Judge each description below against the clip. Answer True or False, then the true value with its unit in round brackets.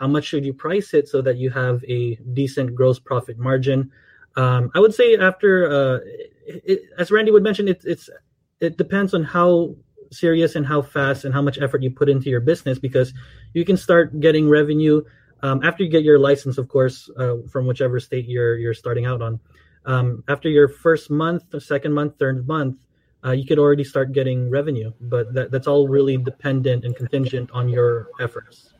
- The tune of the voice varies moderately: True (3.7 semitones)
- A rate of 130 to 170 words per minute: False (200 wpm)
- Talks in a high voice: False (135 Hz)